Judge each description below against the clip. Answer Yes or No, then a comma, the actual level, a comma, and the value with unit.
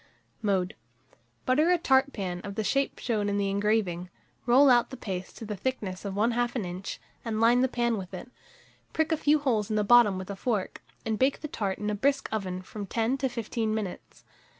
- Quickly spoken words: Yes, fast, 215 wpm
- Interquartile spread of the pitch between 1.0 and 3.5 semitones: No, average, 4.3 semitones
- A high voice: Yes, high, 220 Hz